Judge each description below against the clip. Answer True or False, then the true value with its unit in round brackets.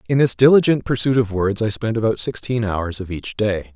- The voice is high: False (110 Hz)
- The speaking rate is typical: False (225 wpm)